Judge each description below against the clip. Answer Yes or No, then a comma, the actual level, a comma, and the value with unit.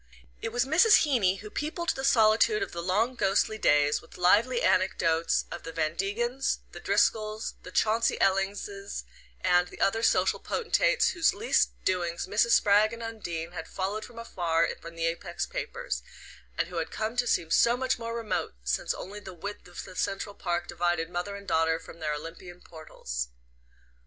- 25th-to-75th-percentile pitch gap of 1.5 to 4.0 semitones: No, average, 5.2 semitones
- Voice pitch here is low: No, high, 195 Hz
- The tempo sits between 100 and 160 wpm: No, average, 175 wpm